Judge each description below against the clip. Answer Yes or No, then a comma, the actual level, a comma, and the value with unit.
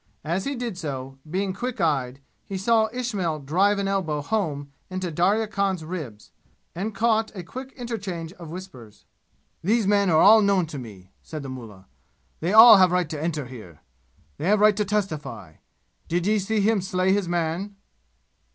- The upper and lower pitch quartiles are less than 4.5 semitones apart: No, average, 5.2 semitones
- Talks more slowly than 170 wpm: No, average, 175 wpm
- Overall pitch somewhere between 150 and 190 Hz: Yes, medium, 185 Hz